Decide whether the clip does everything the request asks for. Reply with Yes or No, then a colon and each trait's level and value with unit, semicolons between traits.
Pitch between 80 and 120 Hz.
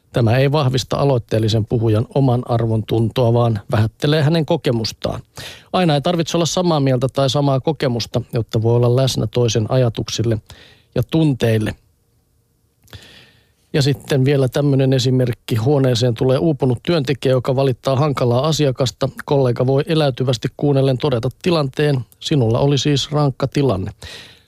No: low, 130 Hz